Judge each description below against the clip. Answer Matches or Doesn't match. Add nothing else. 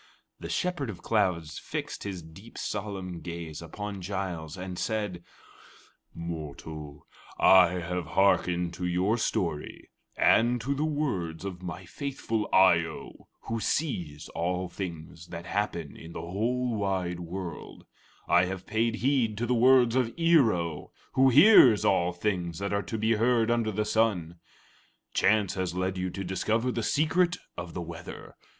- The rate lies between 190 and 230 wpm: Doesn't match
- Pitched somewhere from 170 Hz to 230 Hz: Doesn't match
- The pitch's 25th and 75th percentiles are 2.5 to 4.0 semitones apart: Doesn't match